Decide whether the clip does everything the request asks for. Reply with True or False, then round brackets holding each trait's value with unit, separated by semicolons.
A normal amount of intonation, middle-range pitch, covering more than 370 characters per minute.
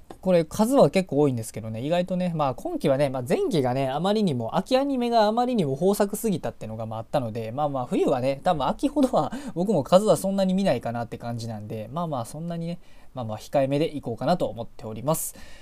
False (8.4 semitones; 150 Hz; 490 characters per minute)